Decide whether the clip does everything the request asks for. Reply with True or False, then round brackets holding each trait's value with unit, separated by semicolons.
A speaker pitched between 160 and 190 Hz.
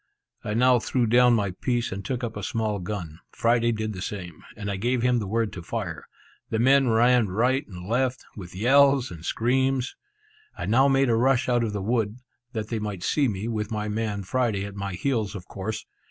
False (110 Hz)